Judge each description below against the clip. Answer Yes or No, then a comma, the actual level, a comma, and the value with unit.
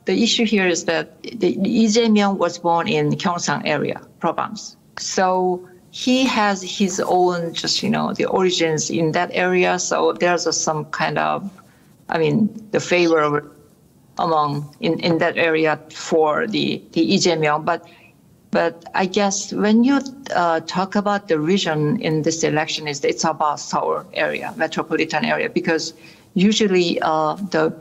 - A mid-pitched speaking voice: Yes, medium, 170 Hz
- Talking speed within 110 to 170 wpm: Yes, average, 155 wpm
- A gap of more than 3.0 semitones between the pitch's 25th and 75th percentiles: Yes, average, 3.5 semitones